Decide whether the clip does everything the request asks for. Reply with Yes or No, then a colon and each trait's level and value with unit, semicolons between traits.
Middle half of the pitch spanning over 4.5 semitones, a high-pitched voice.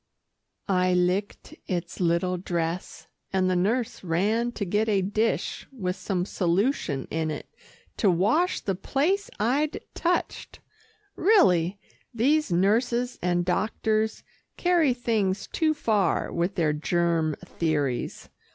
Yes: average, 5.1 semitones; high, 195 Hz